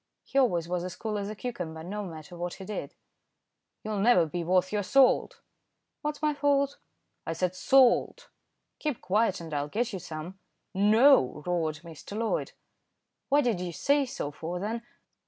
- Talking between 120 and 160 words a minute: No, average, 170 wpm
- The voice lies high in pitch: Yes, high, 195 Hz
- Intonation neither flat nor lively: No, wide, 6.0 semitones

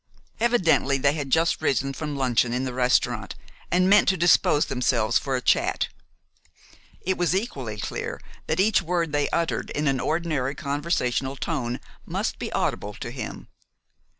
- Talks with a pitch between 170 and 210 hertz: No, medium, 145 Hz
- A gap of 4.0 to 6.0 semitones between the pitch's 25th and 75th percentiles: Yes, average, 4.6 semitones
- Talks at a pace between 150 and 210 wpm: Yes, average, 155 wpm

